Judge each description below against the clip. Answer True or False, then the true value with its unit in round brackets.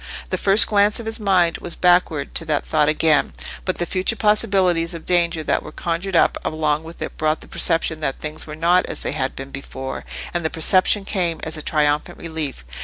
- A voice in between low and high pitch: True (165 Hz)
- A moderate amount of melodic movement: True (3.1 semitones)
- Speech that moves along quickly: True (210 wpm)